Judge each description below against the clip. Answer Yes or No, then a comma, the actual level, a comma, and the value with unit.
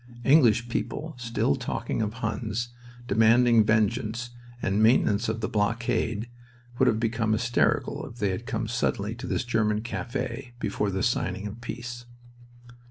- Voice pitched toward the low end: Yes, low, 115 Hz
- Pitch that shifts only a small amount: Yes, narrow, 2.0 semitones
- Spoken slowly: No, average, 145 wpm